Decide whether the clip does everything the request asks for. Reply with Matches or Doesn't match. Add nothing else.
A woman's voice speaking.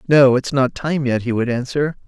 Doesn't match